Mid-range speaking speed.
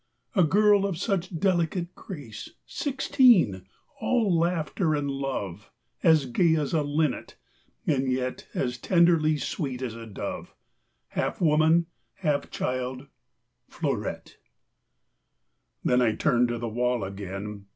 No: slow, 120 wpm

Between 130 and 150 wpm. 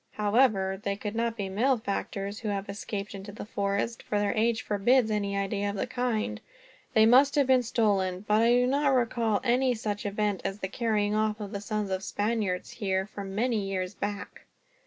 No: average, 195 wpm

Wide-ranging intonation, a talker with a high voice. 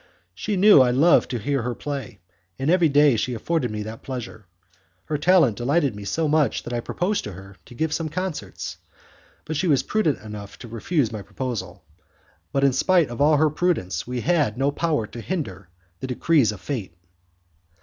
No: wide, 6.0 semitones; low, 135 Hz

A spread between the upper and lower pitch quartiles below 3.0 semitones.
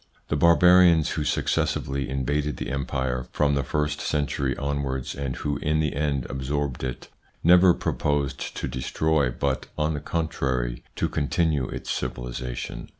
Yes: narrow, 2.5 semitones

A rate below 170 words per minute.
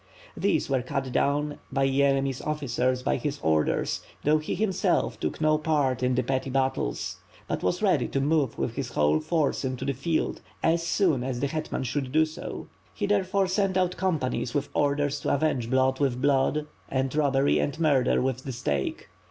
No: average, 185 wpm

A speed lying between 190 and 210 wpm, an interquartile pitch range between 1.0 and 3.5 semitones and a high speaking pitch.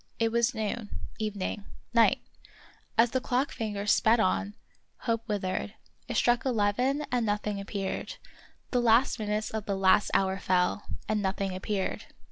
No: average, 160 wpm; average, 2.8 semitones; high, 210 Hz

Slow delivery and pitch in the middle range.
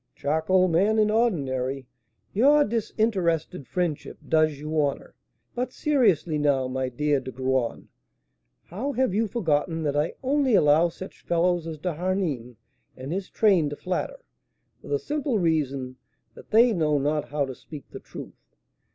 No: average, 150 wpm; medium, 165 Hz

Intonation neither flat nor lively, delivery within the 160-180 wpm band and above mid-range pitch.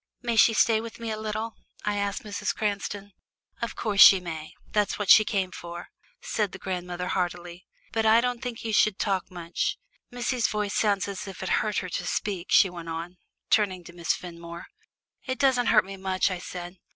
No: average, 3.4 semitones; average, 200 wpm; high, 200 Hz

